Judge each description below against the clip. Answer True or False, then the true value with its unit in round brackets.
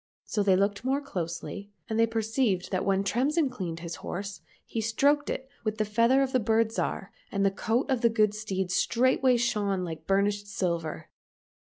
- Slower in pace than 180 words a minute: False (185 wpm)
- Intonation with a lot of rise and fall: False (3.5 semitones)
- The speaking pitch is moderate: False (210 Hz)